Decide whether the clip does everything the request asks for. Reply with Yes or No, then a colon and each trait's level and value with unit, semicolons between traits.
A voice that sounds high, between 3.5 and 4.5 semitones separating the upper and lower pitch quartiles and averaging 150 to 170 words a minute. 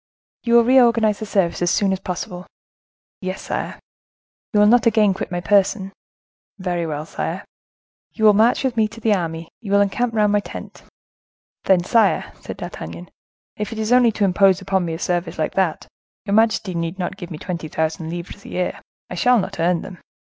No: high, 195 Hz; average, 3.8 semitones; average, 195 wpm